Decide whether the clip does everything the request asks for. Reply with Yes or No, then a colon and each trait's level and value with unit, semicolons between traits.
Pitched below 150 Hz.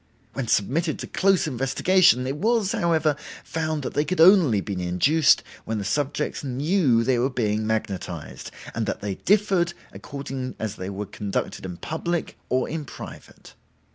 Yes: low, 135 Hz